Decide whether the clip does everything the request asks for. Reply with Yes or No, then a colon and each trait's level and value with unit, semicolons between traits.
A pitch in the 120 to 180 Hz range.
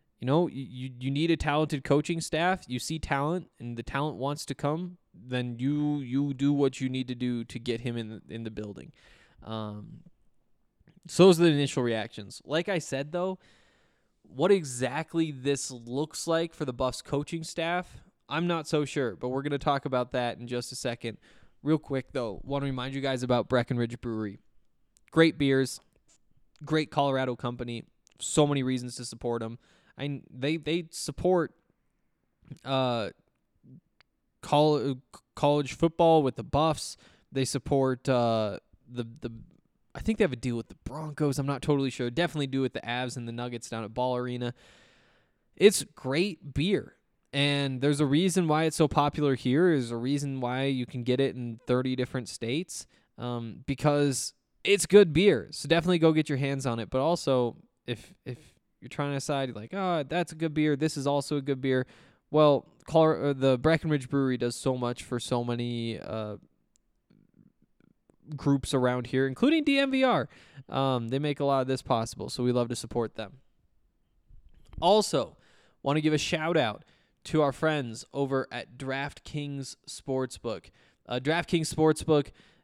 Yes: medium, 140 Hz